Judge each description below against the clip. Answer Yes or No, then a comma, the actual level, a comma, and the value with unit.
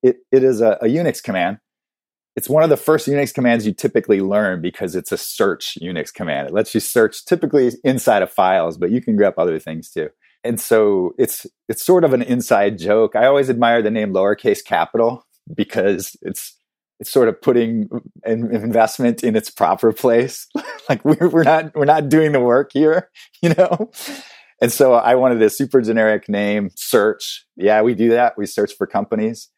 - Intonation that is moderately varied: No, wide, 5.9 semitones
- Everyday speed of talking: Yes, average, 195 wpm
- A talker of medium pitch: No, low, 130 Hz